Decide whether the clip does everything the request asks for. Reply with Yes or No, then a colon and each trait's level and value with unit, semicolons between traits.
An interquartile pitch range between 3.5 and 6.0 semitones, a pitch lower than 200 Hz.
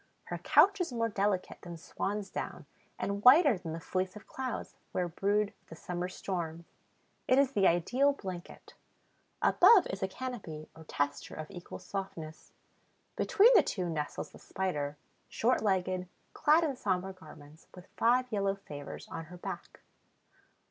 Yes: average, 5.3 semitones; high, 190 Hz